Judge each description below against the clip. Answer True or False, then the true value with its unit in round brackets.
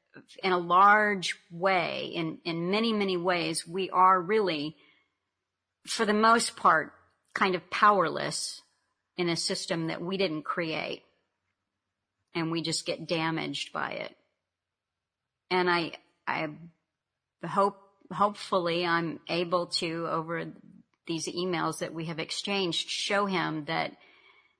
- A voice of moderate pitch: True (175 Hz)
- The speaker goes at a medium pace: False (125 wpm)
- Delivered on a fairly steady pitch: False (3.0 semitones)